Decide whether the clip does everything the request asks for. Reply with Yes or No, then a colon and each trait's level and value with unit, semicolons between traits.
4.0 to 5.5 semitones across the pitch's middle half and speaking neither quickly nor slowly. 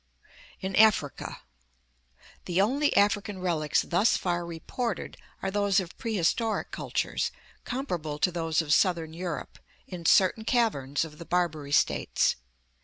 No: average, 4.3 semitones; slow, 130 wpm